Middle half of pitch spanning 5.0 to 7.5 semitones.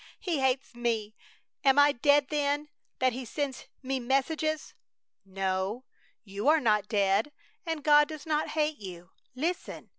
Yes: wide, 5.6 semitones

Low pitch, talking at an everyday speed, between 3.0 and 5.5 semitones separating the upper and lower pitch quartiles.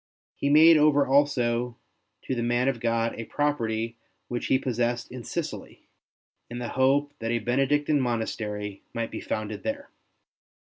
Yes: low, 120 Hz; average, 150 wpm; average, 3.6 semitones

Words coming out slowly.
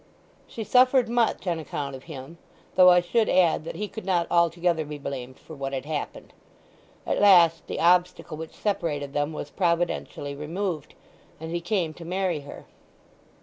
No: average, 170 wpm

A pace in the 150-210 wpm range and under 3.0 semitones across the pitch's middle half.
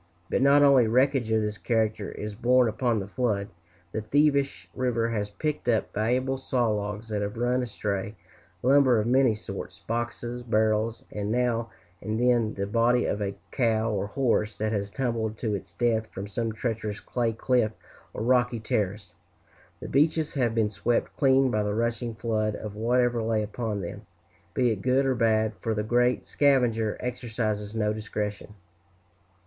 Yes: average, 170 wpm; narrow, 2.5 semitones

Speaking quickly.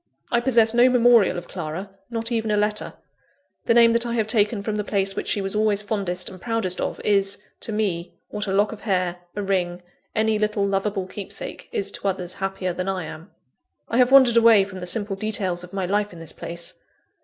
Yes: fast, 215 wpm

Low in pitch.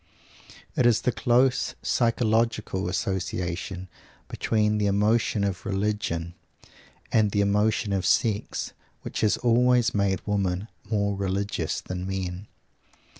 Yes: low, 100 Hz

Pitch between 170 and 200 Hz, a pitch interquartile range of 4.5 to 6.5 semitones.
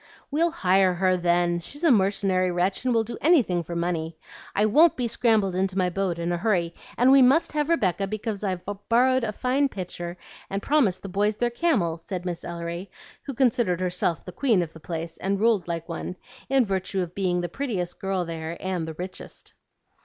Yes: high, 190 Hz; average, 5.0 semitones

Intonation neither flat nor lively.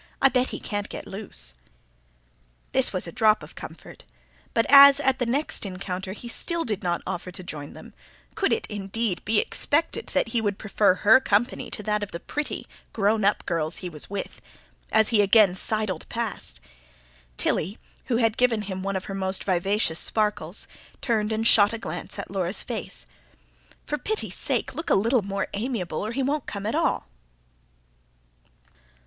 Yes: average, 3.6 semitones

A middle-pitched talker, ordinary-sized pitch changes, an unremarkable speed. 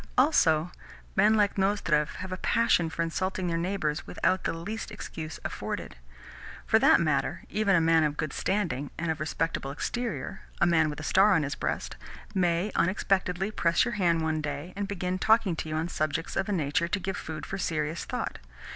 Yes: medium, 170 Hz; average, 3.6 semitones; average, 190 wpm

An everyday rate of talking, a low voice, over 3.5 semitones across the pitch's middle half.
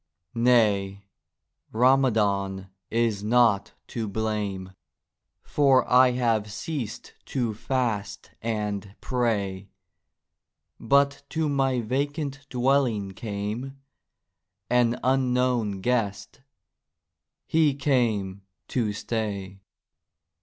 No: slow, 75 wpm; low, 115 Hz; average, 4.1 semitones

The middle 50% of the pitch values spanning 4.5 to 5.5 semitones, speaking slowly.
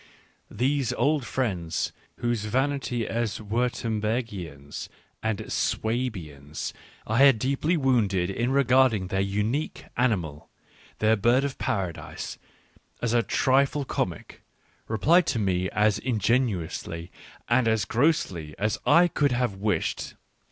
Yes: average, 4.9 semitones; slow, 115 wpm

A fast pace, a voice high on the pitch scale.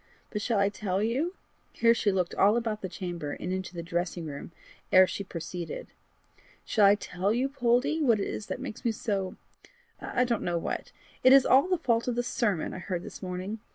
Yes: fast, 210 wpm; high, 205 Hz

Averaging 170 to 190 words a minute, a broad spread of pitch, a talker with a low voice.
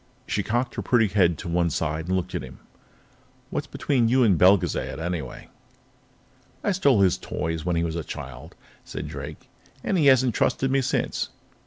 Yes: average, 180 wpm; wide, 6.9 semitones; very low, 95 Hz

